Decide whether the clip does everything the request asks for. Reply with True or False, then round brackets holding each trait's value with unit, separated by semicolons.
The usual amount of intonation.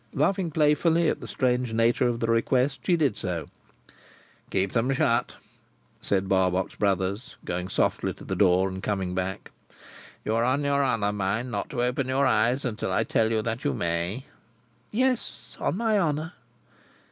False (6.3 semitones)